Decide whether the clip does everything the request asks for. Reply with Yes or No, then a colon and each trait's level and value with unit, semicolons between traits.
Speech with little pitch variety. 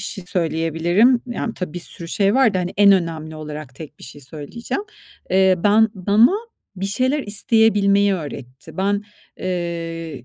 No: average, 4.1 semitones